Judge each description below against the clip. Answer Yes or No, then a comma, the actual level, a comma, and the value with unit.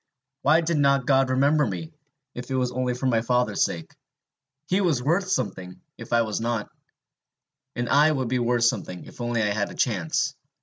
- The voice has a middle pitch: No, low, 125 Hz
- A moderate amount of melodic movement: Yes, average, 3.4 semitones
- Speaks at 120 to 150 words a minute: No, average, 190 wpm